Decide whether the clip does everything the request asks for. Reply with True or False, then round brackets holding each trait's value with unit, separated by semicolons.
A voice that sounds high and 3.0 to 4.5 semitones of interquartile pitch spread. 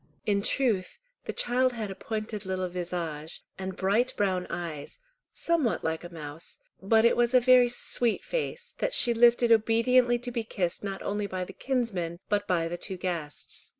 False (205 Hz; 5.0 semitones)